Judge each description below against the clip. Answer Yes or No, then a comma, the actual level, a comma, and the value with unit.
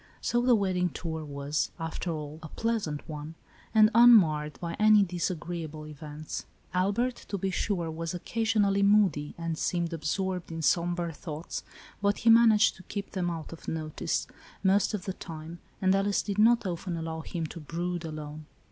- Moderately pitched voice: Yes, medium, 175 Hz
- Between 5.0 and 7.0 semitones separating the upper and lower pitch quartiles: No, average, 4.1 semitones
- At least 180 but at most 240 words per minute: No, average, 165 wpm